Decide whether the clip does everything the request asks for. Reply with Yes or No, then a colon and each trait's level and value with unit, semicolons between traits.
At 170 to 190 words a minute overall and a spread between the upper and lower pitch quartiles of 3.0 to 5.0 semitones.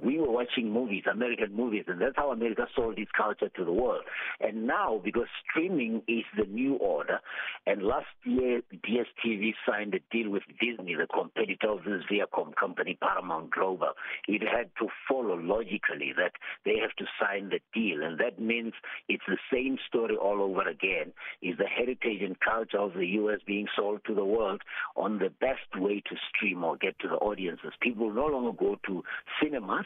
Yes: average, 185 wpm; average, 3.5 semitones